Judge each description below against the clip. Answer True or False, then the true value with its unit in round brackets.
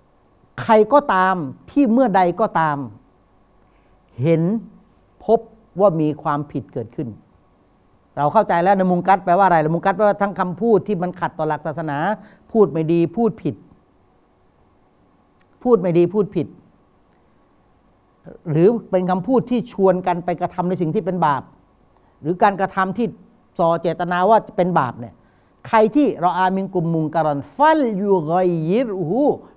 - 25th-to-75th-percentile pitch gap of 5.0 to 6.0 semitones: True (5.5 semitones)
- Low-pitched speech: False (180 Hz)